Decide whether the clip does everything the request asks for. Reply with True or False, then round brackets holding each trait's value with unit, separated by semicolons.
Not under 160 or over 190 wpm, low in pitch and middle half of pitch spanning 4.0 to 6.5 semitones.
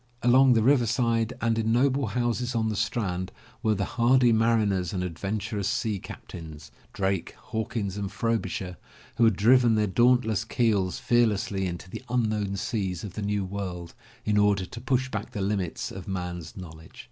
False (170 wpm; 105 Hz; 3.5 semitones)